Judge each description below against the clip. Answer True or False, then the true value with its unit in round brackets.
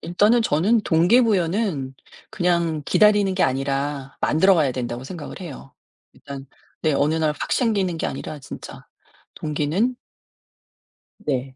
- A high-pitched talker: False (160 Hz)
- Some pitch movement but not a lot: False (5.8 semitones)